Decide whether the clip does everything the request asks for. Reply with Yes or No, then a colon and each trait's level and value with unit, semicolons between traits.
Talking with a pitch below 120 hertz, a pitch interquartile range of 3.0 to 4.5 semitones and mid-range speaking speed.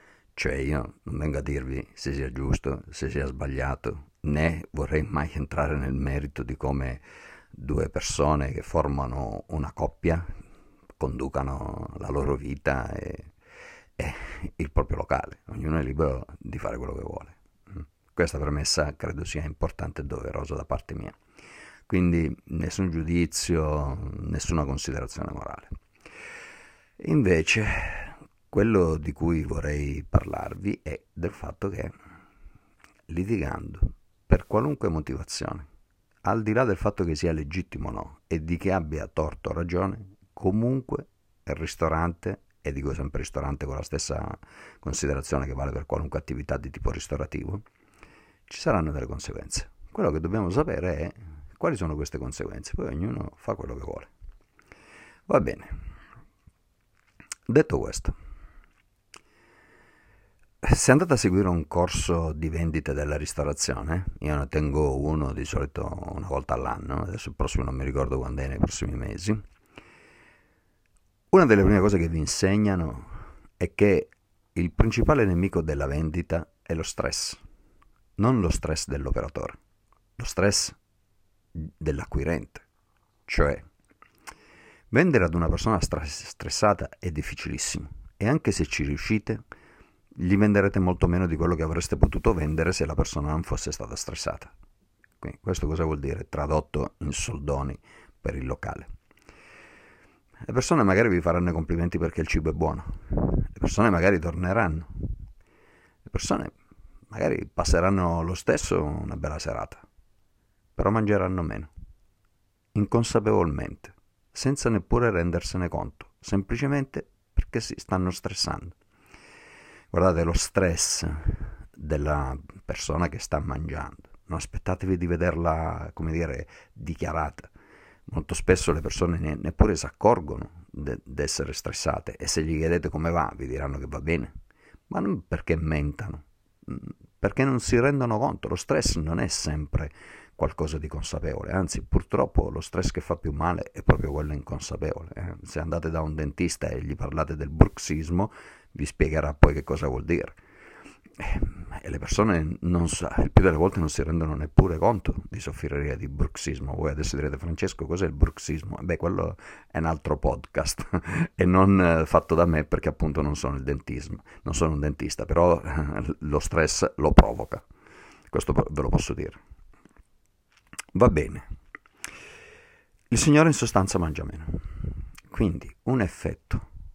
Yes: very low, 80 Hz; average, 4.2 semitones; average, 140 wpm